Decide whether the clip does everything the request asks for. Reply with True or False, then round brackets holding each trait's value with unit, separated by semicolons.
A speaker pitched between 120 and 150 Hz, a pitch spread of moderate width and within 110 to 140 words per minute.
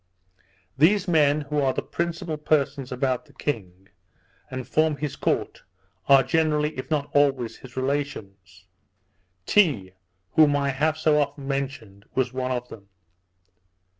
True (140 Hz; 3.0 semitones; 135 wpm)